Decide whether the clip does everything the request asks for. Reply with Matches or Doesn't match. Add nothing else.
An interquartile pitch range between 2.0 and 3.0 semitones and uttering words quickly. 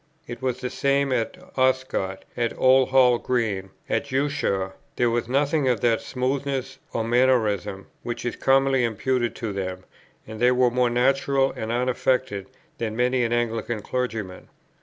Doesn't match